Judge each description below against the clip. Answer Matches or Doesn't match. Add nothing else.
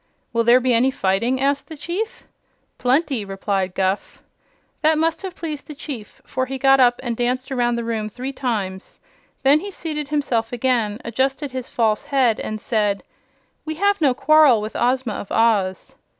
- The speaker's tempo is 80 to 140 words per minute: Doesn't match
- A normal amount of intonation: Matches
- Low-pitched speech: Doesn't match